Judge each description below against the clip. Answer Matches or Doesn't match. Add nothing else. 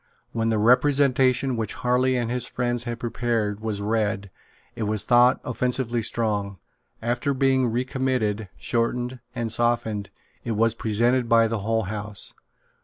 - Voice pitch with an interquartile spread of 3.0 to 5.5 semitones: Doesn't match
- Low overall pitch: Matches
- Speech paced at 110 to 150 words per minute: Matches